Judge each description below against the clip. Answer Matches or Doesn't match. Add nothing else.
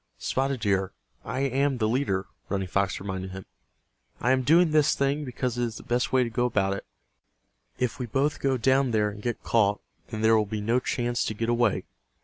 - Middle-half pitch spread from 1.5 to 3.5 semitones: Doesn't match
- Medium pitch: Doesn't match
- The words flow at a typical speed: Doesn't match